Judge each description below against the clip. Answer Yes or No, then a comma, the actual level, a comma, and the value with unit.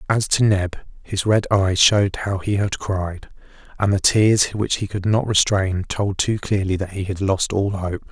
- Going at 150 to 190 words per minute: No, fast, 205 wpm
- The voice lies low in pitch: Yes, low, 100 Hz